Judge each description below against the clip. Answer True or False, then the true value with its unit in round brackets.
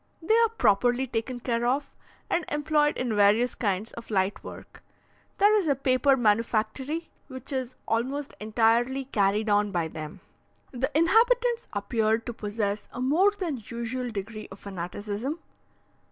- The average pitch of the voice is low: False (240 Hz)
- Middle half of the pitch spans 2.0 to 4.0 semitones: False (5.0 semitones)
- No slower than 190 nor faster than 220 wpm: False (145 wpm)